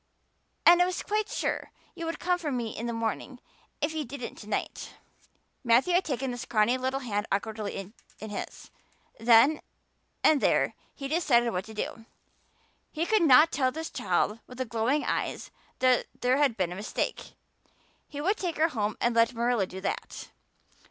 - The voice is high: Yes, very high, 250 Hz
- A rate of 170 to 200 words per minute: Yes, average, 180 wpm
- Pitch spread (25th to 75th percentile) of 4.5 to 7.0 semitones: Yes, average, 5.3 semitones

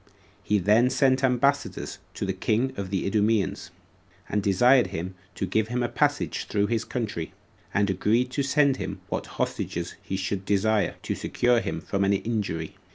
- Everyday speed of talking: Yes, average, 170 wpm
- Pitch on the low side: Yes, low, 105 Hz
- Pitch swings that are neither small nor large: Yes, average, 4.1 semitones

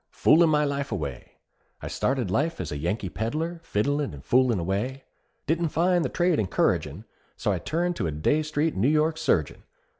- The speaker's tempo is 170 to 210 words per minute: Yes, average, 180 wpm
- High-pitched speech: No, medium, 140 Hz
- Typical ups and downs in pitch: No, wide, 8.2 semitones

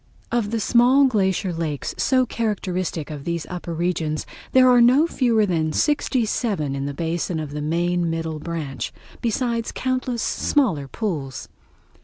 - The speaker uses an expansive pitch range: Yes, wide, 7.1 semitones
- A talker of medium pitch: Yes, medium, 180 Hz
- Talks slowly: No, average, 150 wpm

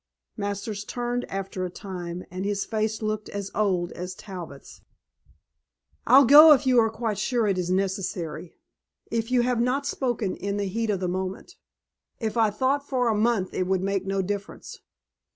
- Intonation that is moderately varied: Yes, average, 3.8 semitones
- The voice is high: Yes, high, 205 Hz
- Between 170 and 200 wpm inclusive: Yes, average, 175 wpm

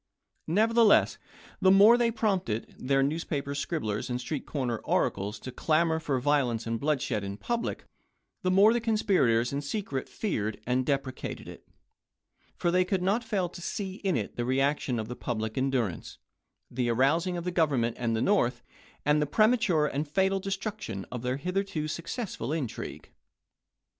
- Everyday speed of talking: Yes, average, 165 wpm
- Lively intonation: Yes, wide, 7.5 semitones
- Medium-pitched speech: Yes, medium, 150 Hz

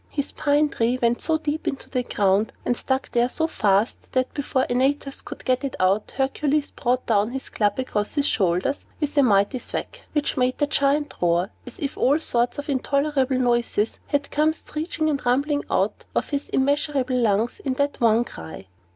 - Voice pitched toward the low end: No, very high, 260 Hz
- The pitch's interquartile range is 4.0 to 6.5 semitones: No, average, 3.5 semitones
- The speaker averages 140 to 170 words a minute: No, average, 185 wpm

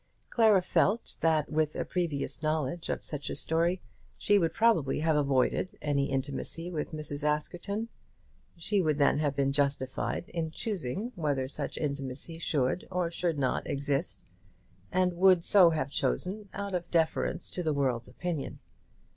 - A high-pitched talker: No, medium, 160 Hz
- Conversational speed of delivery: Yes, average, 155 wpm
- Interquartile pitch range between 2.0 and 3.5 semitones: No, average, 4.1 semitones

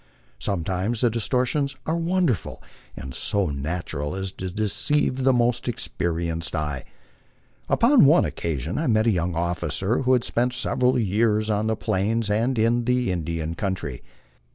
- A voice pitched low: Yes, low, 105 Hz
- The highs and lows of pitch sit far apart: Yes, wide, 6.3 semitones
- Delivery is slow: No, average, 155 wpm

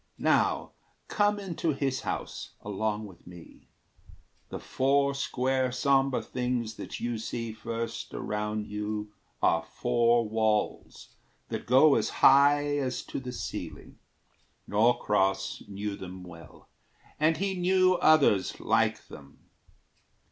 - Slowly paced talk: Yes, slow, 120 wpm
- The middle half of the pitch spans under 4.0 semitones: No, average, 4.8 semitones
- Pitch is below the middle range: Yes, low, 120 Hz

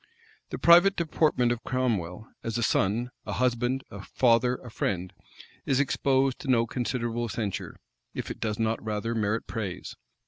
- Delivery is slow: No, average, 160 wpm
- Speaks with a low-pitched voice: Yes, low, 120 Hz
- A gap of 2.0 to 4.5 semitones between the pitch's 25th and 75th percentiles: Yes, average, 2.8 semitones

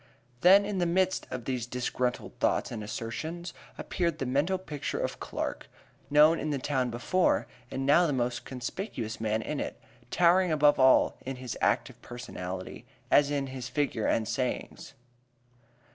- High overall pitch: No, low, 135 Hz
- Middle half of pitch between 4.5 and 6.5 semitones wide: Yes, wide, 5.5 semitones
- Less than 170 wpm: Yes, average, 160 wpm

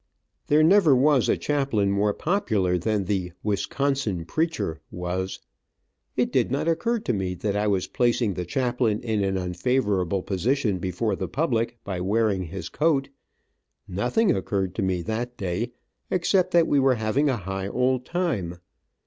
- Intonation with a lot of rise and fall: Yes, wide, 6.3 semitones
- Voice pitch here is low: Yes, low, 110 Hz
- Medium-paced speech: Yes, average, 155 wpm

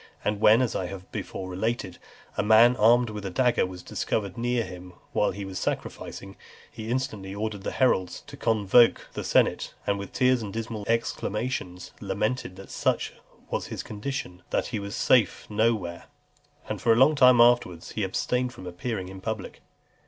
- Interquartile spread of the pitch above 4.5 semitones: No, average, 3.8 semitones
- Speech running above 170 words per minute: Yes, average, 180 wpm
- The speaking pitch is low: Yes, low, 105 Hz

